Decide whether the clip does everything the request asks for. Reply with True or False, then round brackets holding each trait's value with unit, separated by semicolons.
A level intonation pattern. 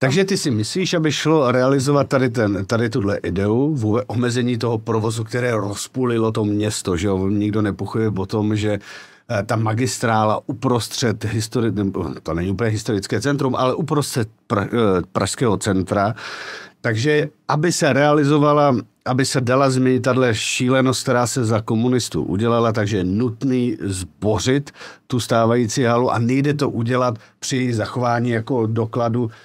False (3.4 semitones)